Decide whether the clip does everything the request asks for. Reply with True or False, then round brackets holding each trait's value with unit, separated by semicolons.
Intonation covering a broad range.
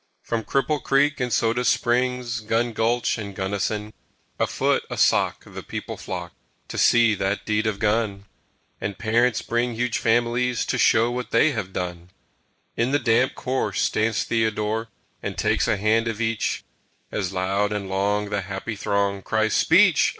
False (2.8 semitones)